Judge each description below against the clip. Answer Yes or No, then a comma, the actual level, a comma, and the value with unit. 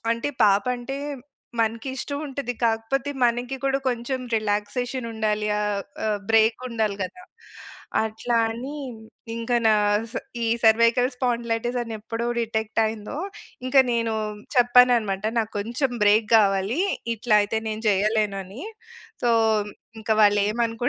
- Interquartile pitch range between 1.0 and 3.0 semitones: Yes, narrow, 2.5 semitones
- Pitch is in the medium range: No, high, 225 Hz